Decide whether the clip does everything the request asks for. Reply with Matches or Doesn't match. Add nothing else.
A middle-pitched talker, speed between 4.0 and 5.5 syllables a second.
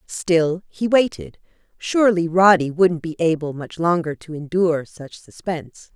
Matches